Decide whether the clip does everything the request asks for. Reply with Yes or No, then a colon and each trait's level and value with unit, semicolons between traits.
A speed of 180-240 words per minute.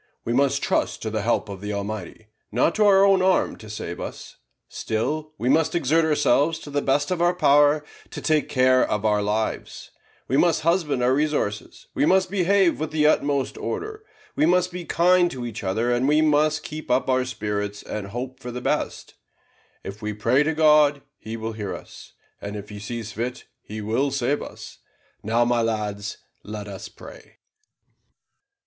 Yes: average, 185 wpm